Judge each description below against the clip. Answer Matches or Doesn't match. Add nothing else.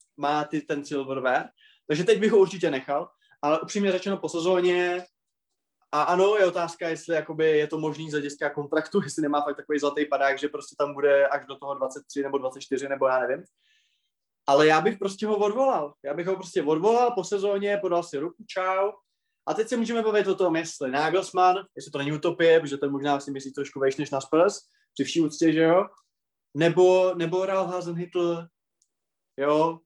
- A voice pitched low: Doesn't match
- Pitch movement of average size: Matches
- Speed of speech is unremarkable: Doesn't match